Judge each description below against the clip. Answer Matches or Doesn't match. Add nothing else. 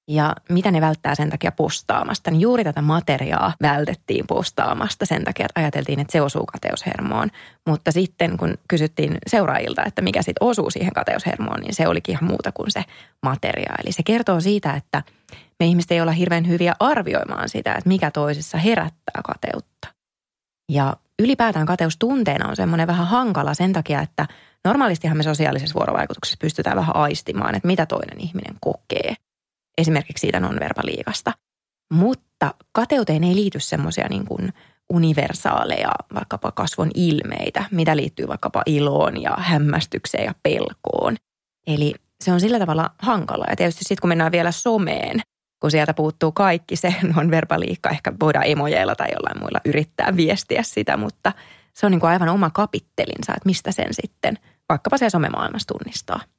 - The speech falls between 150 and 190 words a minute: Matches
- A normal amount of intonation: Matches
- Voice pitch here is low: Doesn't match